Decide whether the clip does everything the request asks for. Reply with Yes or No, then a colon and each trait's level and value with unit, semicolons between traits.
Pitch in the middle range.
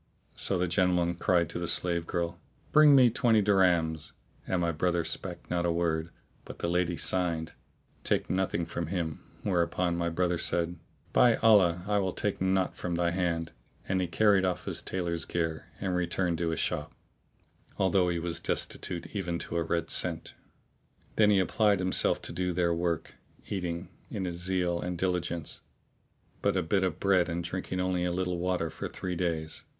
No: very low, 90 Hz